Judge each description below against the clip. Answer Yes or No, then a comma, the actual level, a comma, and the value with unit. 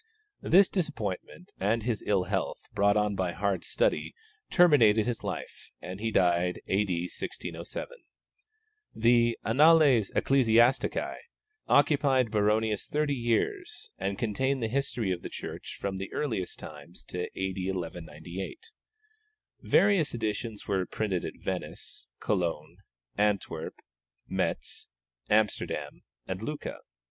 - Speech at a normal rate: No, slow, 115 wpm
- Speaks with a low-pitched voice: Yes, low, 110 Hz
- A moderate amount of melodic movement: No, wide, 5.9 semitones